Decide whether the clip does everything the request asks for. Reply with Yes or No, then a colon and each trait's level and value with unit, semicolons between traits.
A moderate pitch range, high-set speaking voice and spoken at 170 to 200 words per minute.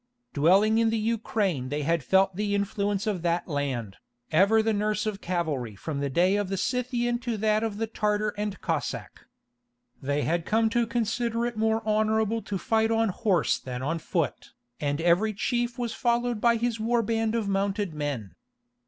Yes: average, 4.8 semitones; high, 210 Hz; average, 180 wpm